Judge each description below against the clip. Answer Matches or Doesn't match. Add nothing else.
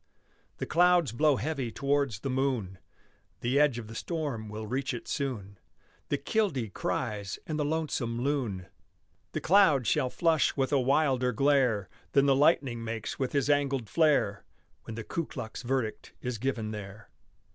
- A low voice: Matches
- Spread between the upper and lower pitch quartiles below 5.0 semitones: Matches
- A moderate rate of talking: Matches